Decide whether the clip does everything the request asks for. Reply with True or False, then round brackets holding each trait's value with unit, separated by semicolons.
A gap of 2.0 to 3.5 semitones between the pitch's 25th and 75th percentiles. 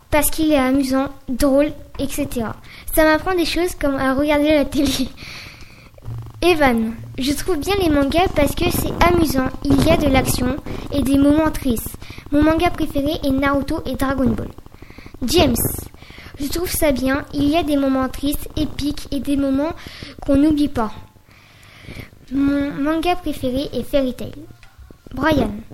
True (2.7 semitones)